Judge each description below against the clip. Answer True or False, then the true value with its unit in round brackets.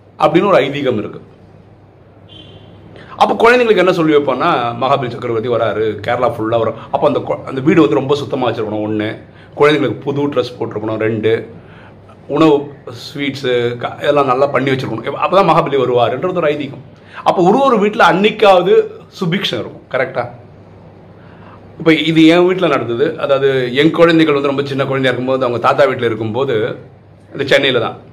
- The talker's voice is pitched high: False (135 Hz)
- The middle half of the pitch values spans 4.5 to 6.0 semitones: True (5.6 semitones)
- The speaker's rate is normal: False (145 wpm)